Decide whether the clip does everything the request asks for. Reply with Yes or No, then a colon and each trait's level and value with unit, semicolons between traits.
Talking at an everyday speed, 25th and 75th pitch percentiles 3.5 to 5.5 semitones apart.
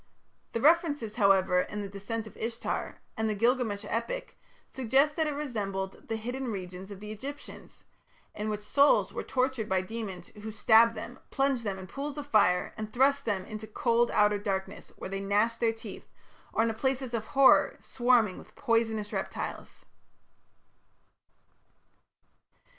Yes: average, 155 wpm; average, 3.8 semitones